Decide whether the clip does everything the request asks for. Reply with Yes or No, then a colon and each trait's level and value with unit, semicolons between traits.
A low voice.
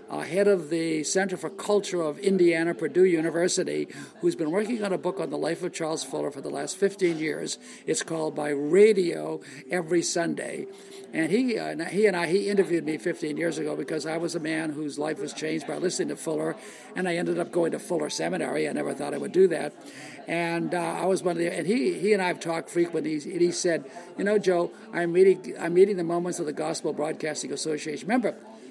No: medium, 170 Hz